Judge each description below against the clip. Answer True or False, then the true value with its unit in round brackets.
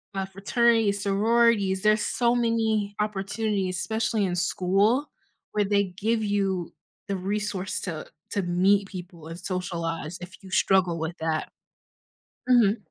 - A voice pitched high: True (195 Hz)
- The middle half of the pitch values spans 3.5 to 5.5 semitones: False (2.7 semitones)